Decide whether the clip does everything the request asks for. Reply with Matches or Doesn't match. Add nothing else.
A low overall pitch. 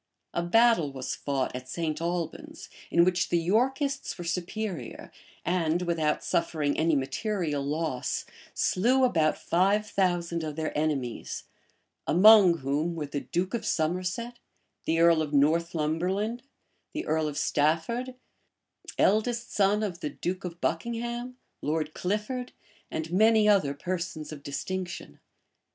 Doesn't match